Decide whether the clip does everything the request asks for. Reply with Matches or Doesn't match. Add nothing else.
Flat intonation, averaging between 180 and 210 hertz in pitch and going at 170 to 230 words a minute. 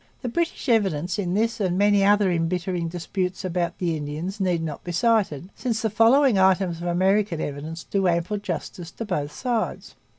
Doesn't match